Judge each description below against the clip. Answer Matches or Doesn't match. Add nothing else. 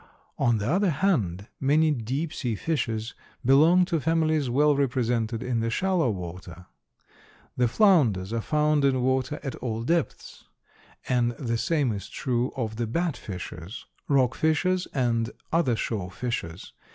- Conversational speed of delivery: Matches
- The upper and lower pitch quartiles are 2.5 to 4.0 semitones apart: Doesn't match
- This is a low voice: Matches